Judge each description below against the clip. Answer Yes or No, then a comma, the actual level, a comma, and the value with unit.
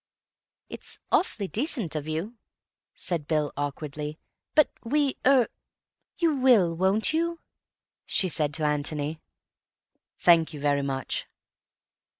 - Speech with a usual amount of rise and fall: No, wide, 8.7 semitones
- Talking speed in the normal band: No, slow, 110 wpm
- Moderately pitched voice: Yes, medium, 165 Hz